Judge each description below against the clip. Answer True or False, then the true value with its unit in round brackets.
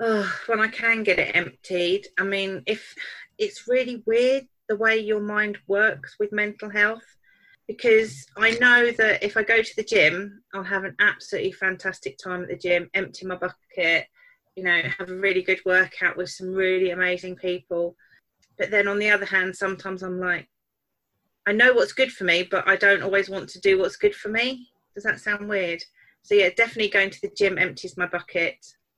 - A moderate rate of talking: True (195 wpm)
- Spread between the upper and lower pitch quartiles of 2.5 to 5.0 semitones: True (3.3 semitones)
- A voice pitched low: False (200 Hz)